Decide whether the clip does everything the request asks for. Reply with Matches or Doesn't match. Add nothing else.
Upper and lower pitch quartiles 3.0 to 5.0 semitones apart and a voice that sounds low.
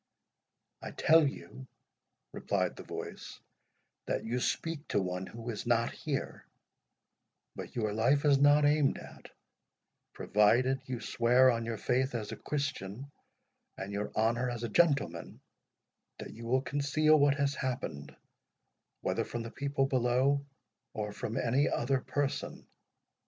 Matches